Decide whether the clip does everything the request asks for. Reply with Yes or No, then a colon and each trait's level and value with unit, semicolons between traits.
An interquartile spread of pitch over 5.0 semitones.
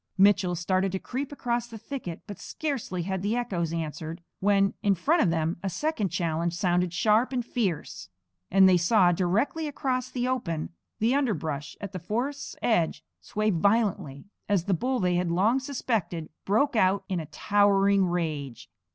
Yes: wide, 5.4 semitones